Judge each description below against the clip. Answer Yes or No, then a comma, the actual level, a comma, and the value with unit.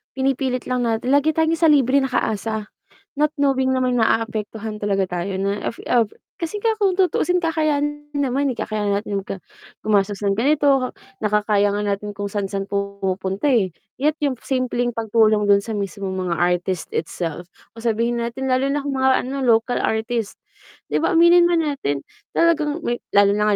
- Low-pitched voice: No, high, 230 Hz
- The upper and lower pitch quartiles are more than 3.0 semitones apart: Yes, wide, 5.4 semitones